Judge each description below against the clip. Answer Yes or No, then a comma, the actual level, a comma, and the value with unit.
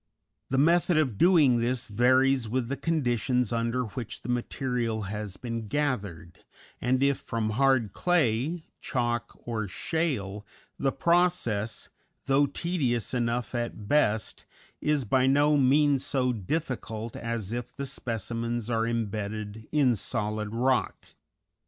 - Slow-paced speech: Yes, slow, 125 wpm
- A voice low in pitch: Yes, low, 120 Hz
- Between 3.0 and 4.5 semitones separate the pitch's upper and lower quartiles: Yes, average, 3.6 semitones